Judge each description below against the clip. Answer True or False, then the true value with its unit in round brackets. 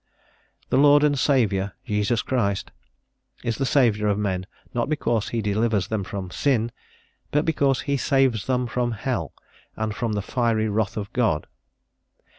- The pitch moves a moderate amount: True (4.0 semitones)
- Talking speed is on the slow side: False (155 wpm)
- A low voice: True (115 Hz)